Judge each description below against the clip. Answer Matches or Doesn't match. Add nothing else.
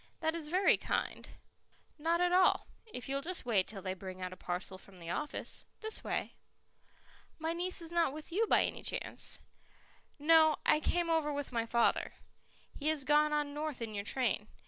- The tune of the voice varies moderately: Doesn't match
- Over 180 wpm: Matches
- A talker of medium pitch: Doesn't match